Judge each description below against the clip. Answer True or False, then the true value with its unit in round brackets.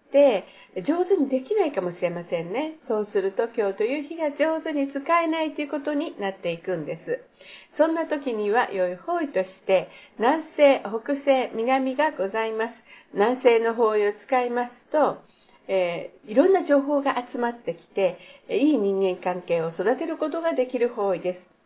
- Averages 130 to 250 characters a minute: False (330 characters per minute)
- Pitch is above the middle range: True (245 Hz)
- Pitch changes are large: True (7.0 semitones)